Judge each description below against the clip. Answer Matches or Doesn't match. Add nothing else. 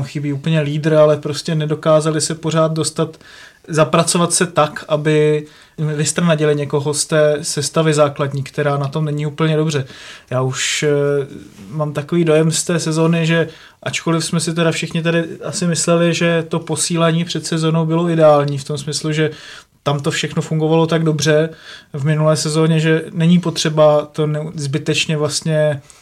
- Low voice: Doesn't match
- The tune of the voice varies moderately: Doesn't match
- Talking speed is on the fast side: Doesn't match